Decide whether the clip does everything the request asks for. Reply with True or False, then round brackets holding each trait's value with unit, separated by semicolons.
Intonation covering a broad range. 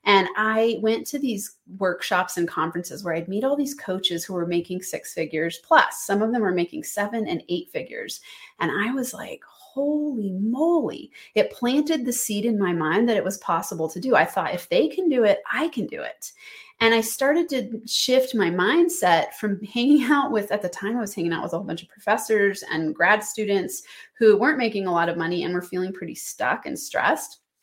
True (6.0 semitones)